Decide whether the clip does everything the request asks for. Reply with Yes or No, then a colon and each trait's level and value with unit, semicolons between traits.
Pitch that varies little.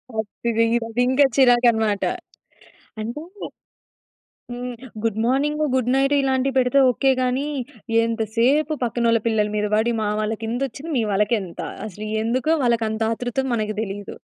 No: average, 3.0 semitones